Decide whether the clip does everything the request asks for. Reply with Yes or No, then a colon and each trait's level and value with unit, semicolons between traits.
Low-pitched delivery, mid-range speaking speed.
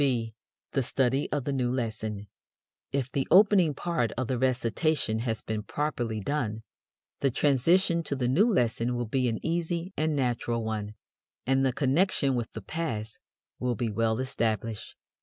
Yes: low, 125 Hz; average, 160 wpm